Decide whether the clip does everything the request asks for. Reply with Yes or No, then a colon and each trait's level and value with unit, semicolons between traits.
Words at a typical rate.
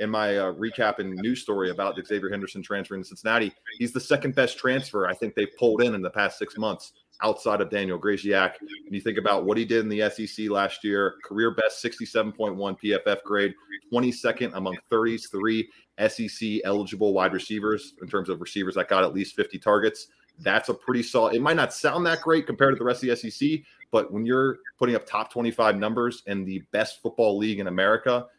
No: fast, 210 wpm